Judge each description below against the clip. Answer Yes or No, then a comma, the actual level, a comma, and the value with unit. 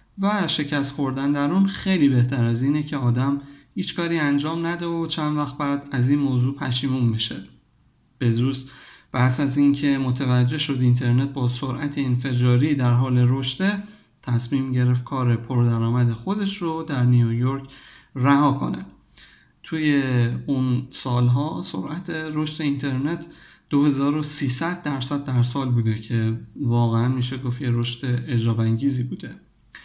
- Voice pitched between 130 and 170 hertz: Yes, low, 135 Hz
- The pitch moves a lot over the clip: No, average, 2.9 semitones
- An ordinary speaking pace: Yes, average, 135 wpm